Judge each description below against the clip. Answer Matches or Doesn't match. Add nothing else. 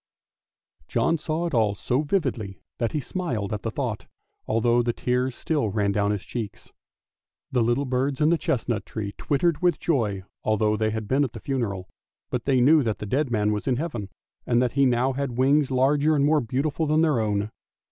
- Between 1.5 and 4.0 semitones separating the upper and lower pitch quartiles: Doesn't match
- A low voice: Matches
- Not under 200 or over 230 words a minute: Matches